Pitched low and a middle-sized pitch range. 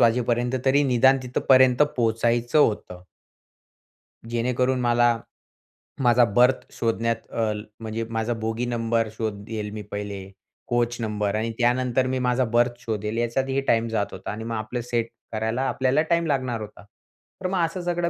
No: low, 120 Hz; narrow, 2.2 semitones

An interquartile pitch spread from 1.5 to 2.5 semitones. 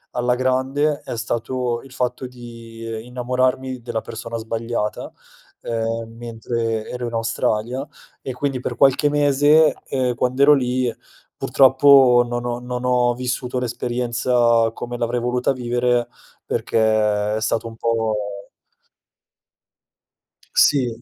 Yes: narrow, 1.8 semitones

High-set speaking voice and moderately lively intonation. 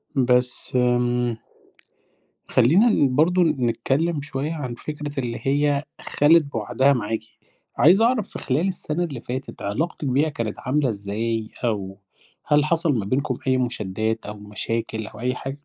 No: low, 130 Hz; average, 4.5 semitones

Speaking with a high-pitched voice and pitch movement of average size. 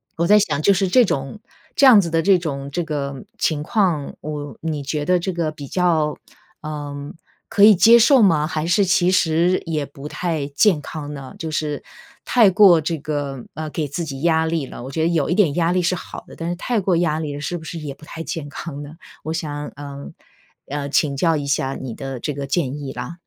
No: medium, 155 Hz; average, 3.4 semitones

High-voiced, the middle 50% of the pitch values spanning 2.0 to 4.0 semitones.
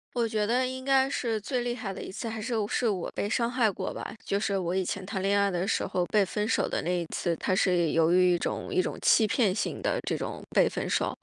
No: high, 205 Hz; average, 4.4 semitones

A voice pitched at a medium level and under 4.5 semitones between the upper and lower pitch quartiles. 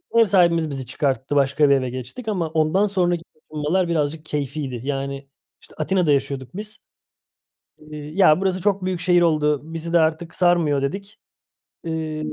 Yes: medium, 155 Hz; average, 3.7 semitones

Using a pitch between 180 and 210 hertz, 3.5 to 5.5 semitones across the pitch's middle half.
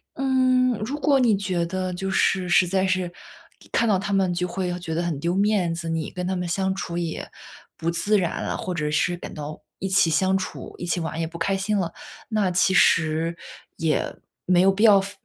No: medium, 185 Hz; narrow, 2.4 semitones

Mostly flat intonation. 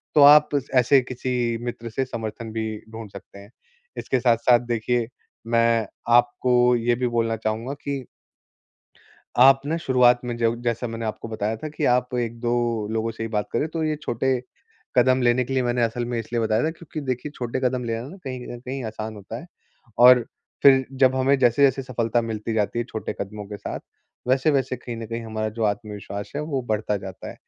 Yes: narrow, 2.3 semitones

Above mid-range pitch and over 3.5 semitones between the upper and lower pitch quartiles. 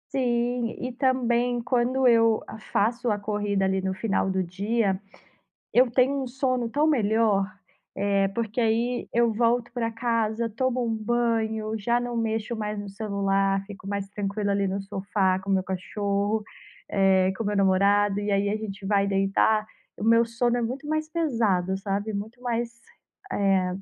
No: high, 220 Hz; average, 3.2 semitones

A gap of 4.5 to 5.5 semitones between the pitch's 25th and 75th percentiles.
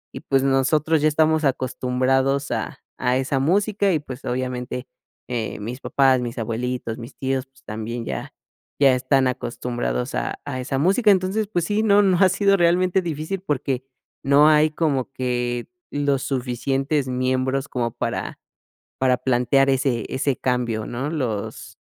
No: average, 3.5 semitones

